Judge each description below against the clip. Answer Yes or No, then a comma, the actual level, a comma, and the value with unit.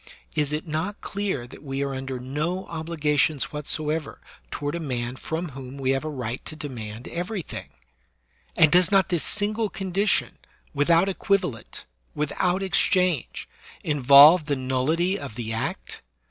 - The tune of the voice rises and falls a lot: No, average, 4.8 semitones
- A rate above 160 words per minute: No, average, 145 wpm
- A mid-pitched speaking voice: Yes, medium, 150 Hz